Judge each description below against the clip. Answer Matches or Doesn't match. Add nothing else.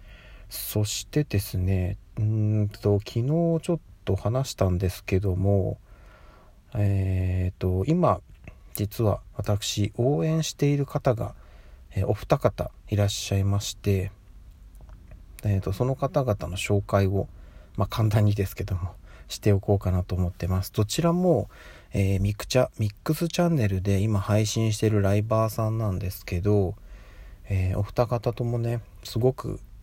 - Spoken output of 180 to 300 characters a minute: Matches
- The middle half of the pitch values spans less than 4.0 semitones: Matches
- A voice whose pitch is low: Matches